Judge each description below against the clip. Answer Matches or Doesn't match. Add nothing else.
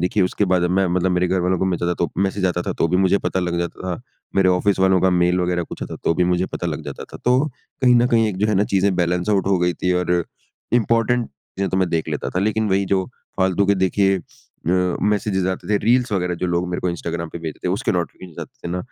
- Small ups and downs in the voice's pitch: Matches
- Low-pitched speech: Matches